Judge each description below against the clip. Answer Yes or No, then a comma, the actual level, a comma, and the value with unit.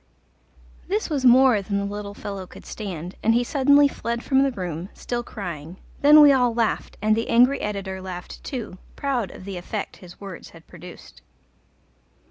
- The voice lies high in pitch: Yes, high, 210 Hz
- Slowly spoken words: No, average, 175 wpm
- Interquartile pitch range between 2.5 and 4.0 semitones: No, average, 5.3 semitones